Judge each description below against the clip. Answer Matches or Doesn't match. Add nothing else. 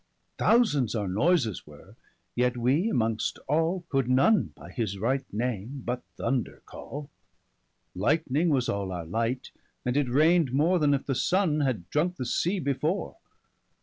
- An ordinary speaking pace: Matches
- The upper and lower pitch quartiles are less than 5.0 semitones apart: Doesn't match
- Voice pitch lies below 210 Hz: Matches